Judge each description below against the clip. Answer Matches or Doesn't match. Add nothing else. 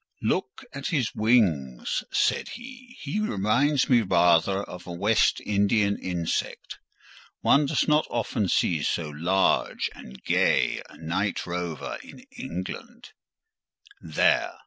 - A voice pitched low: Matches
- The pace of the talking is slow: Matches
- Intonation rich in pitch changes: Matches